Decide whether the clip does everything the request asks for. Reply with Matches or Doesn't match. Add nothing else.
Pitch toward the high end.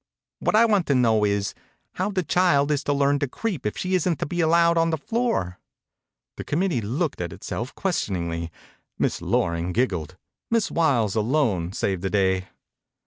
Doesn't match